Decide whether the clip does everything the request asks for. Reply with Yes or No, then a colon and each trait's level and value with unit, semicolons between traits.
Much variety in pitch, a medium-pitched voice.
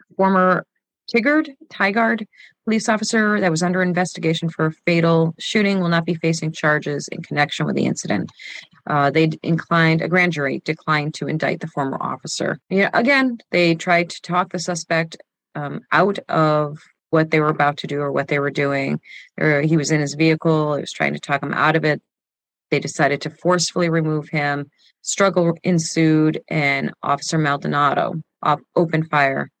No: average, 3.1 semitones; medium, 160 Hz